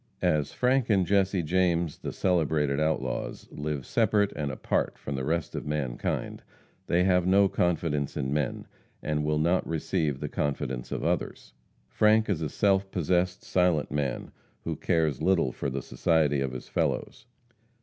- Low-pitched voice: Yes, very low, 80 Hz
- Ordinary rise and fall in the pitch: Yes, average, 4.1 semitones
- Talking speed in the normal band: Yes, average, 160 wpm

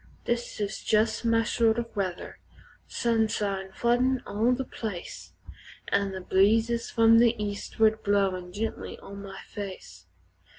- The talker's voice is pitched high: Yes, high, 215 Hz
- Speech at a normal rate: No, slow, 130 wpm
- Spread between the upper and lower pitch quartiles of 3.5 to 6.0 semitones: No, narrow, 2.6 semitones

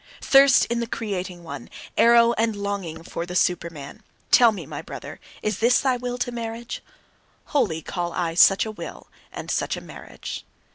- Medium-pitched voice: No, high, 215 Hz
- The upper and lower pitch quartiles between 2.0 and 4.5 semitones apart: No, average, 5.3 semitones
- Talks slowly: No, average, 175 wpm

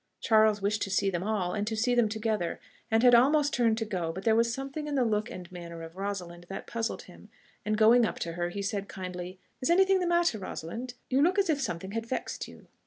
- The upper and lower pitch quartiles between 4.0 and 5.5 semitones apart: Yes, average, 4.6 semitones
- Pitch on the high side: Yes, high, 215 Hz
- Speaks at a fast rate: Yes, fast, 245 wpm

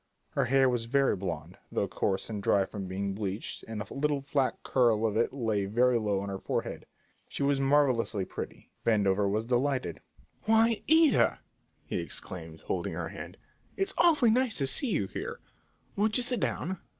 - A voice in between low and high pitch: No, low, 120 Hz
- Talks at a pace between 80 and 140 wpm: No, average, 175 wpm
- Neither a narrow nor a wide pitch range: No, wide, 6.4 semitones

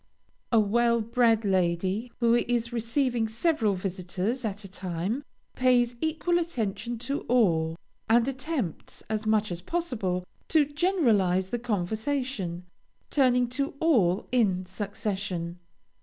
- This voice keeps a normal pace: No, slow, 120 wpm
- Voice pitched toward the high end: Yes, high, 225 Hz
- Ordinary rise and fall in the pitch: Yes, average, 4.9 semitones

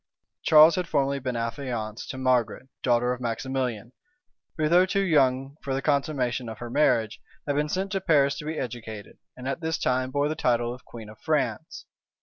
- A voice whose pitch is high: No, low, 130 Hz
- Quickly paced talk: No, average, 190 wpm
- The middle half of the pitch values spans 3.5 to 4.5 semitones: Yes, average, 4.0 semitones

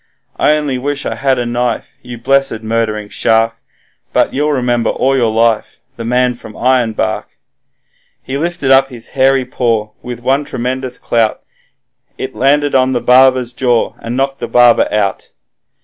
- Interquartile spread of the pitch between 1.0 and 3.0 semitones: Yes, narrow, 2.5 semitones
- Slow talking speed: No, average, 160 wpm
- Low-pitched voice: Yes, low, 125 Hz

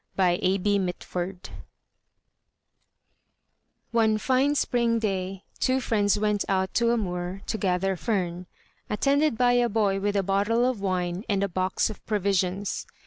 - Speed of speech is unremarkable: Yes, average, 145 wpm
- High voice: Yes, high, 200 Hz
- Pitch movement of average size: Yes, average, 3.5 semitones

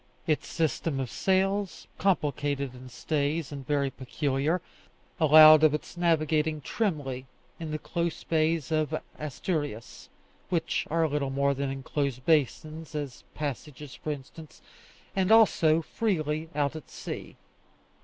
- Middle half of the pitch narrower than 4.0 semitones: Yes, narrow, 2.5 semitones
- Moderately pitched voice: Yes, medium, 150 Hz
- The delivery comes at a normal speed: No, slow, 125 wpm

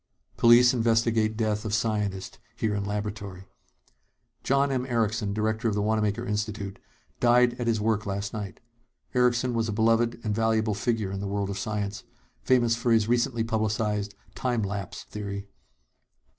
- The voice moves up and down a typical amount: No, narrow, 2.1 semitones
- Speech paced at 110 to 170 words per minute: Yes, average, 155 wpm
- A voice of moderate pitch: No, low, 110 Hz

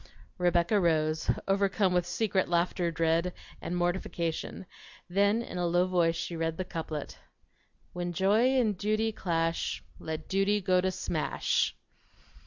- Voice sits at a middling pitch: Yes, medium, 180 Hz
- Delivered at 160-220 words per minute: No, slow, 135 wpm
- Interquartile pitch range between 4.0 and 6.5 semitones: No, average, 2.7 semitones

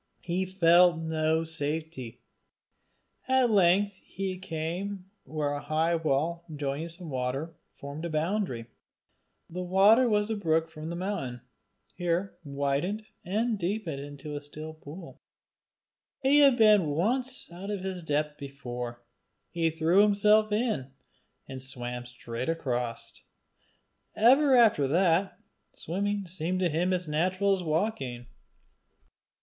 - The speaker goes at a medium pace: No, slow, 125 wpm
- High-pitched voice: No, medium, 170 Hz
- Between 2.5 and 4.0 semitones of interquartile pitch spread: No, average, 5.1 semitones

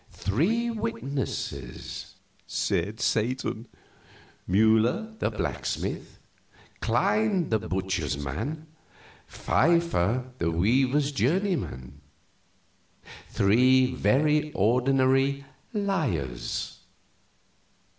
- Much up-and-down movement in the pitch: Yes, wide, 7.5 semitones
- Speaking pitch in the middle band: No, low, 130 Hz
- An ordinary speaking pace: No, slow, 65 wpm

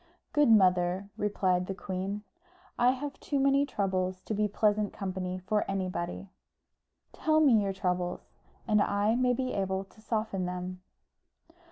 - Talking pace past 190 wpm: No, average, 145 wpm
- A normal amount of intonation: Yes, average, 3.1 semitones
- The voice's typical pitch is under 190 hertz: No, high, 200 Hz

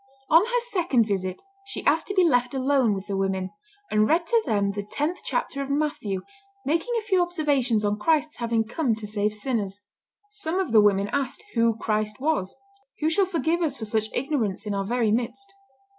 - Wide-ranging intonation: Yes, wide, 7.3 semitones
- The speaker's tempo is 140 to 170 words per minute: No, average, 195 wpm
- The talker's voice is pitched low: No, high, 245 Hz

